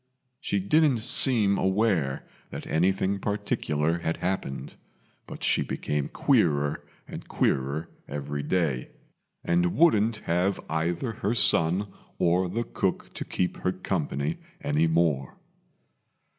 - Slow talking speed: Yes, slow, 115 wpm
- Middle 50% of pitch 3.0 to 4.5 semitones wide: No, average, 5.3 semitones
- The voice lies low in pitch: Yes, very low, 85 Hz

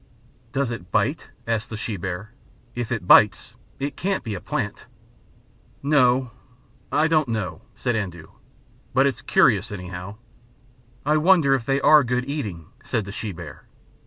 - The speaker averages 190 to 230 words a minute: No, average, 155 wpm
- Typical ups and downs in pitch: No, wide, 5.7 semitones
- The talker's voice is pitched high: No, low, 115 Hz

